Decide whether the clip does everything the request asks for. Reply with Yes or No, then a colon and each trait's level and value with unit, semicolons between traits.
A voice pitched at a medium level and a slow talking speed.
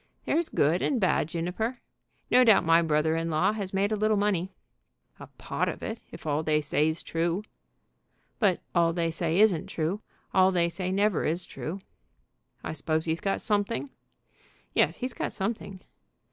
No: medium, 180 Hz; average, 170 wpm